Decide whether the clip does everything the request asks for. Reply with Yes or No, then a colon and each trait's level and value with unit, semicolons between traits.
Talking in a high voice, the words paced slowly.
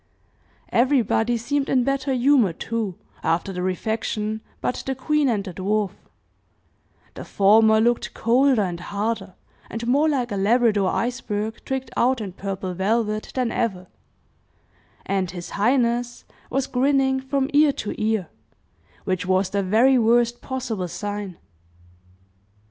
Yes: high, 225 Hz; slow, 130 wpm